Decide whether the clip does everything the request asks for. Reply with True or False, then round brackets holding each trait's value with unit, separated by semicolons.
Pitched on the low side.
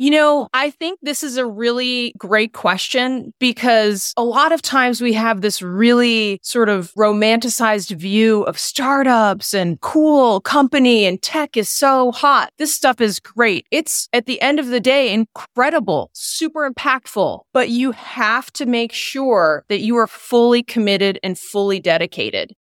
False (240 Hz)